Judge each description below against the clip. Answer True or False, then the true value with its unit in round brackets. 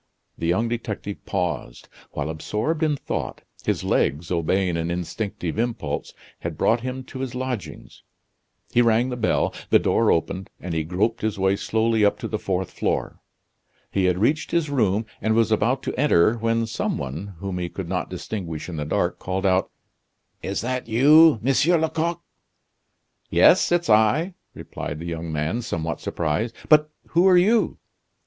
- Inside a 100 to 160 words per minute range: False (170 wpm)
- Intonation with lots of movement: True (6.2 semitones)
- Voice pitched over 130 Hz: False (110 Hz)